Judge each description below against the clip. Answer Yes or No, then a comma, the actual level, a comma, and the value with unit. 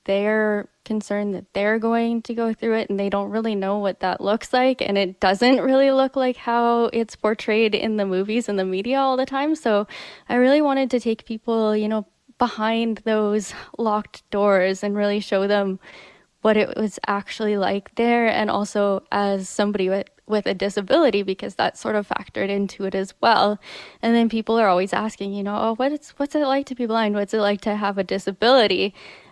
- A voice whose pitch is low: No, high, 215 Hz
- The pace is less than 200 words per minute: No, fast, 205 wpm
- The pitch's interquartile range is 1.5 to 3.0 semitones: Yes, narrow, 2.6 semitones